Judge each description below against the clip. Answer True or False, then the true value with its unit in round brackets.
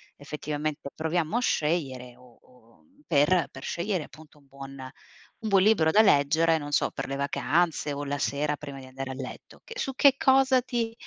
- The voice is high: False (150 Hz)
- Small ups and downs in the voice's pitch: False (4.4 semitones)